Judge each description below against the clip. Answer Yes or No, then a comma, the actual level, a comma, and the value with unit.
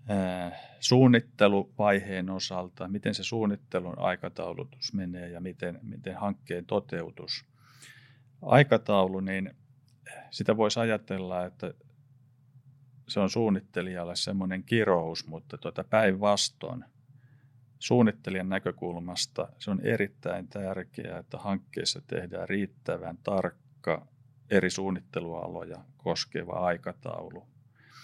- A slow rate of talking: Yes, slow, 90 wpm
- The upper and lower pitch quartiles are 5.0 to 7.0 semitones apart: Yes, wide, 5.4 semitones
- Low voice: Yes, low, 105 Hz